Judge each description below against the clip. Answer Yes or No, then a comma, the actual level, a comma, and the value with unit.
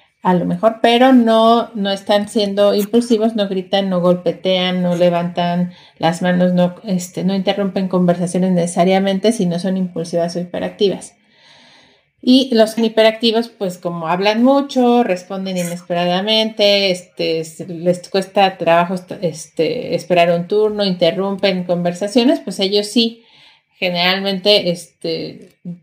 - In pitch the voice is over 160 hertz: Yes, high, 190 Hz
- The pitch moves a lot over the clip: No, average, 3.0 semitones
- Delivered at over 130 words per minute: No, slow, 125 wpm